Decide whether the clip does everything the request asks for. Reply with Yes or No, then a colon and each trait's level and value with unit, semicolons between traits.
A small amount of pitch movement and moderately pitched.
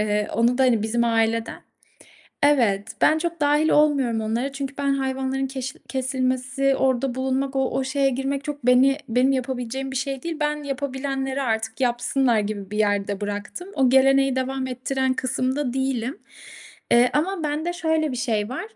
No: narrow, 2.3 semitones; very high, 265 Hz